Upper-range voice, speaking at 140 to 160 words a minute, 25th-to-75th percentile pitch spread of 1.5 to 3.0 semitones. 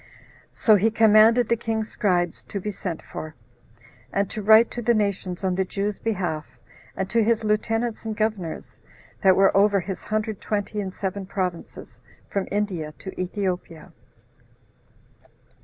Yes: high, 205 Hz; average, 150 wpm; average, 2.7 semitones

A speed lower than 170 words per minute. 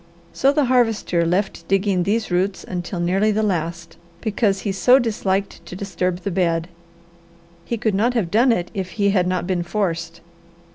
No: average, 175 wpm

